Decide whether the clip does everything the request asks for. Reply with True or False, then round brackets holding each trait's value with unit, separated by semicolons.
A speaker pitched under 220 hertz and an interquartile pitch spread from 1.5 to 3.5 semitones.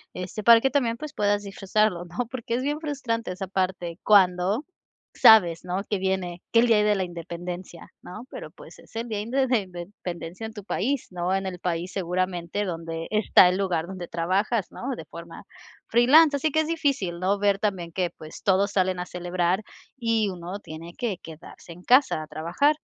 False (190 Hz; 4.4 semitones)